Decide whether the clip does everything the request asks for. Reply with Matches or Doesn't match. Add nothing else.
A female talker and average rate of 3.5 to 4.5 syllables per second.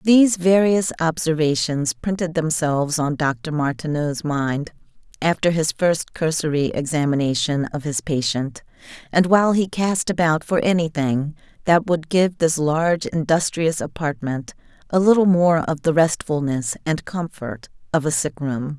Matches